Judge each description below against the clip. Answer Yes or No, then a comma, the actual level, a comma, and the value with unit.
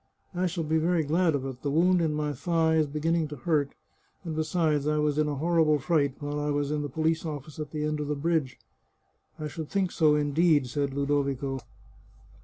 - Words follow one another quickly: Yes, fast, 220 wpm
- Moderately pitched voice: Yes, medium, 150 Hz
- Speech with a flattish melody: Yes, narrow, 2.0 semitones